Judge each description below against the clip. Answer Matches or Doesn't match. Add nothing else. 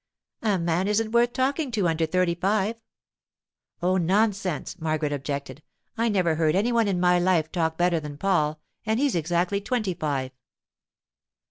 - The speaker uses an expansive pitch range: Doesn't match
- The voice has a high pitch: Doesn't match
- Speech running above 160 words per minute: Doesn't match